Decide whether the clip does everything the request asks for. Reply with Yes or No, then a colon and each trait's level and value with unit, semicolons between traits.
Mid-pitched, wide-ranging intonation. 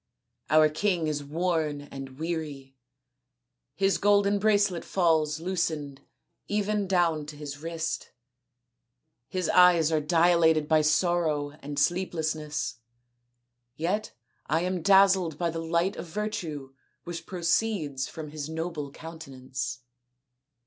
No: medium, 160 Hz; average, 3.2 semitones